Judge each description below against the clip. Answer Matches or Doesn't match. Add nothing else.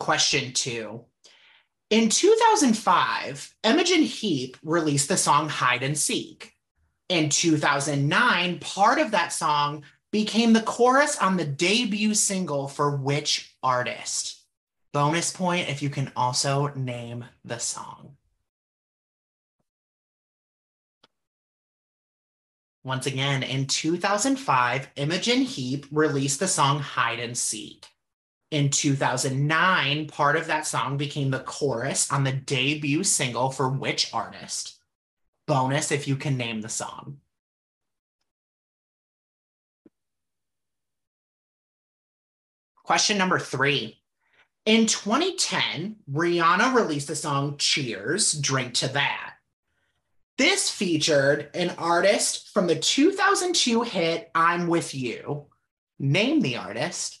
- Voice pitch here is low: Doesn't match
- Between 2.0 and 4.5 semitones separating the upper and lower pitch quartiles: Doesn't match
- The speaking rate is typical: Doesn't match